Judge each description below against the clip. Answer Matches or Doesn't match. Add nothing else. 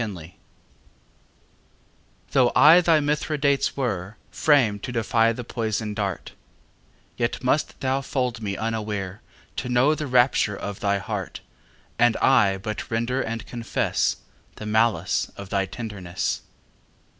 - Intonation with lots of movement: Doesn't match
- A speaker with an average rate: Doesn't match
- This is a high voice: Doesn't match